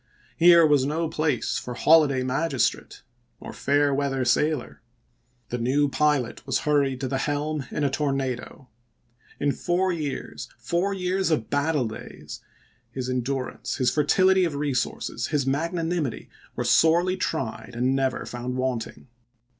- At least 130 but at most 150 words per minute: Yes, average, 145 wpm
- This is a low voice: No, medium, 145 Hz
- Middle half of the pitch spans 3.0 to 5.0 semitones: Yes, average, 3.7 semitones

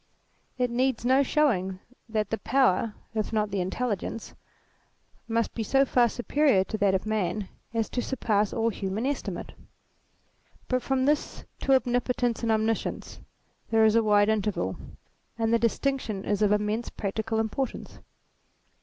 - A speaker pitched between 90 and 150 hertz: No, high, 225 Hz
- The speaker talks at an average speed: Yes, average, 150 wpm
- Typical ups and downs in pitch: Yes, average, 3.0 semitones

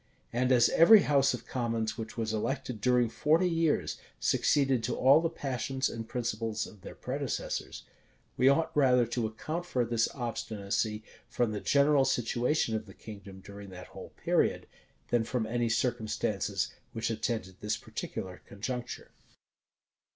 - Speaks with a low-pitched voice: Yes, low, 120 Hz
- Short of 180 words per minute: Yes, average, 150 wpm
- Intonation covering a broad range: No, average, 3.5 semitones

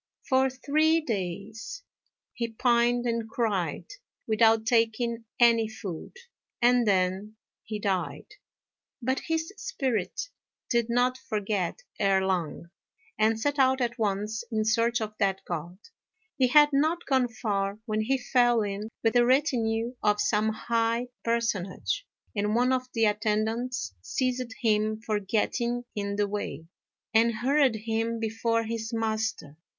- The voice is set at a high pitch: Yes, high, 225 Hz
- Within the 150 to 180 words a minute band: No, slow, 135 wpm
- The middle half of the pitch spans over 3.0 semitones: No, average, 2.7 semitones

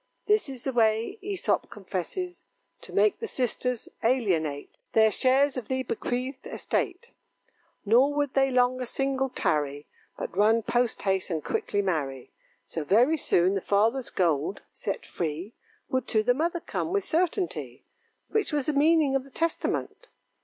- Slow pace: No, average, 155 wpm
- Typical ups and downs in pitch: No, wide, 6.4 semitones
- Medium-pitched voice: No, very high, 250 Hz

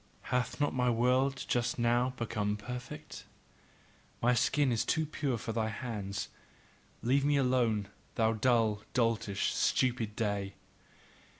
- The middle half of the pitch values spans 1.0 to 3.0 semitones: Yes, average, 2.7 semitones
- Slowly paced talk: Yes, slow, 125 wpm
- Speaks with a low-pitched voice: Yes, low, 120 Hz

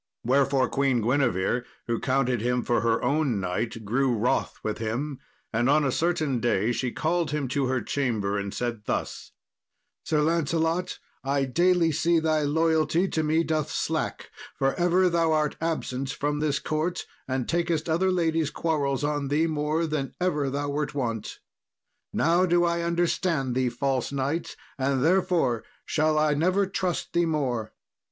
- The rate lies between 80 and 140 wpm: No, average, 160 wpm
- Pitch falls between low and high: Yes, medium, 145 Hz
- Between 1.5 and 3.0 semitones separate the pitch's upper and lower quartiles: No, average, 4.1 semitones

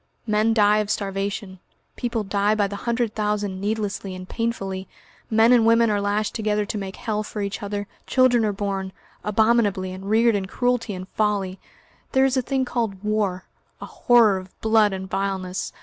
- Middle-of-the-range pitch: No, high, 210 Hz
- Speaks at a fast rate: No, average, 180 wpm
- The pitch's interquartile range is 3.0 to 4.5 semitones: No, narrow, 2.4 semitones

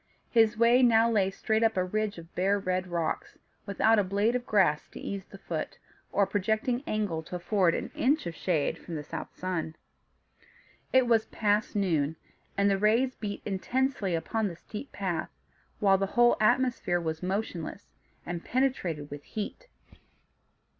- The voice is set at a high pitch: Yes, high, 200 Hz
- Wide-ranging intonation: No, average, 4.2 semitones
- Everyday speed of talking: Yes, average, 165 wpm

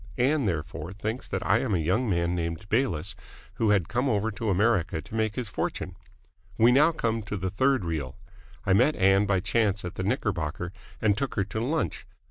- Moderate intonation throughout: Yes, average, 4.3 semitones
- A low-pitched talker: Yes, low, 105 Hz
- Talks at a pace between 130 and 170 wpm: No, average, 200 wpm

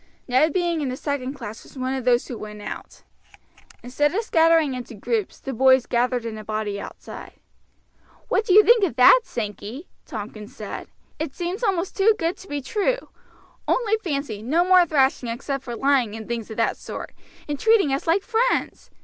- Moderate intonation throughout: No, wide, 6.8 semitones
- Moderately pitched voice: No, very high, 270 Hz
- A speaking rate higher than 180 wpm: Yes, average, 190 wpm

